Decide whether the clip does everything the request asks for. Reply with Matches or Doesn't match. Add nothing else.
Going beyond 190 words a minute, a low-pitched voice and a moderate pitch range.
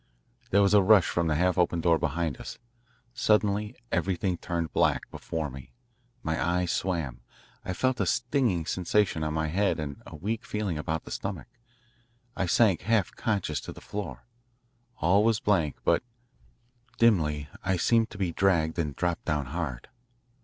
Doesn't match